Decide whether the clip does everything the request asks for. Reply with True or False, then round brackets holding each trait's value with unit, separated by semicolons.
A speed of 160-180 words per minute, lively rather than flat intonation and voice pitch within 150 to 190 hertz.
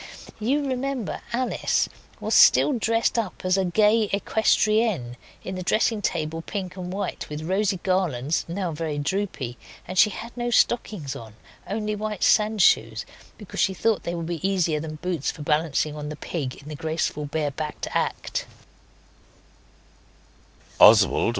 False (150 wpm; 5.7 semitones; 185 Hz)